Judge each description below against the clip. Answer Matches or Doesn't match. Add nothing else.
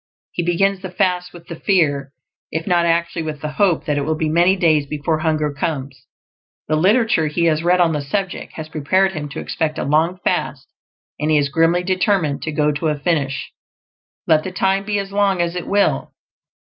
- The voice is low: Doesn't match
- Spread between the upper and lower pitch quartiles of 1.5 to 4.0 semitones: Matches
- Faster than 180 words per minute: Matches